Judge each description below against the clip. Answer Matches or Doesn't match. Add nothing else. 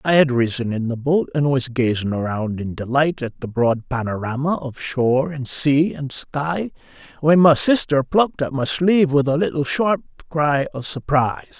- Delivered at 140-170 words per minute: Doesn't match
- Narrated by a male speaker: Matches